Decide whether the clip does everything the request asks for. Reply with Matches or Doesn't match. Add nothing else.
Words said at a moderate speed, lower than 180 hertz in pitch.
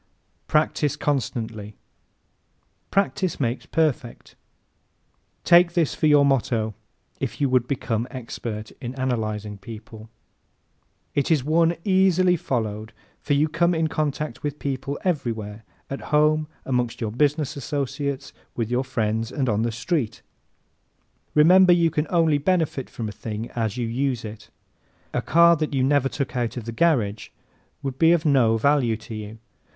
Matches